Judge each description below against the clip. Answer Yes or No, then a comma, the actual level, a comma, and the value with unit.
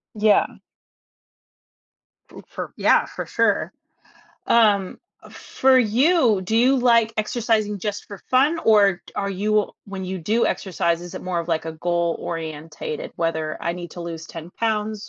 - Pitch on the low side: No, high, 205 Hz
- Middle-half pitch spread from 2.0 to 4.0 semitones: No, average, 4.8 semitones